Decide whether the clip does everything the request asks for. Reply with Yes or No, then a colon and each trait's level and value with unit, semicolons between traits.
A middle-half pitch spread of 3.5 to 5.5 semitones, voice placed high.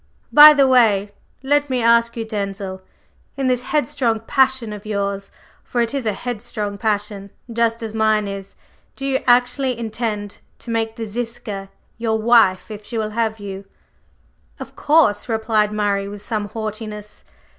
No: narrow, 2.6 semitones; high, 220 Hz